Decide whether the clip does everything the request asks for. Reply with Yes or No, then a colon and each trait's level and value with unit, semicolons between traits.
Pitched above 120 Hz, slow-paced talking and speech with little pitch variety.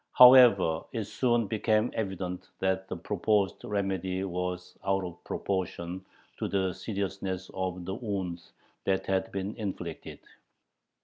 No: very low, 95 Hz; slow, 125 wpm; narrow, 2.1 semitones